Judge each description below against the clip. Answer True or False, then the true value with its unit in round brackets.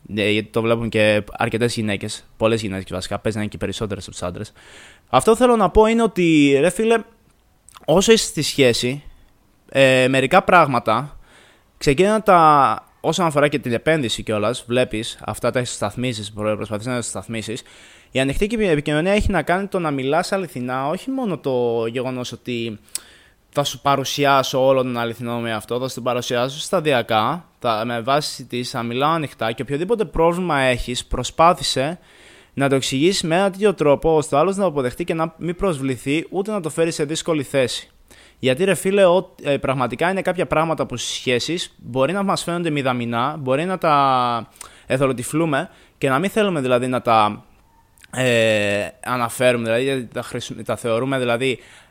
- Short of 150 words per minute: False (170 wpm)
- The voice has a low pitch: True (130 Hz)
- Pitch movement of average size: False (5.9 semitones)